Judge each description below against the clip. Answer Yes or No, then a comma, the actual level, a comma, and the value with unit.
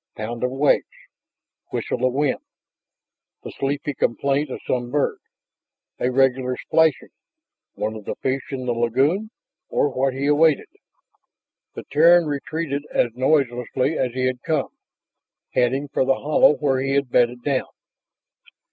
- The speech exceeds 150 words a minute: No, average, 140 wpm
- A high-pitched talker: No, low, 135 Hz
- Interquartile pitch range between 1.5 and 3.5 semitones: Yes, narrow, 2.5 semitones